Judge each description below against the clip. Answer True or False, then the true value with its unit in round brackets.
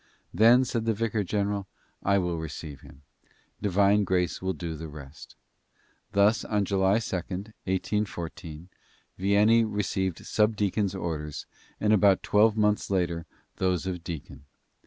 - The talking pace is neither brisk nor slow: False (130 wpm)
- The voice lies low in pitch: True (95 Hz)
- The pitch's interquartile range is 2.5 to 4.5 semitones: True (3.3 semitones)